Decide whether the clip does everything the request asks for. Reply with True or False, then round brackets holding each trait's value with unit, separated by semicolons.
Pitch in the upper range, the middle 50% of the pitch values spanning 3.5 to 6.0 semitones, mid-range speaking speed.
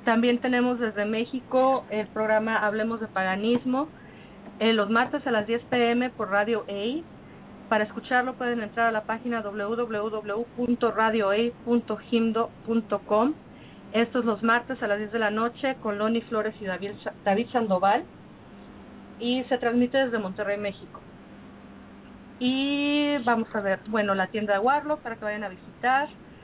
False (225 Hz; 2.5 semitones; 145 wpm)